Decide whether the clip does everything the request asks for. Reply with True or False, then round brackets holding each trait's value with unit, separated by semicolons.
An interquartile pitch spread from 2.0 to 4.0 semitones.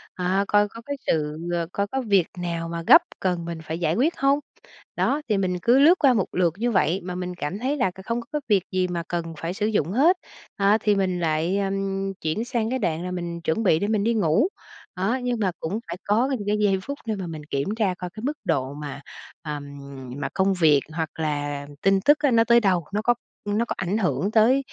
False (4.8 semitones)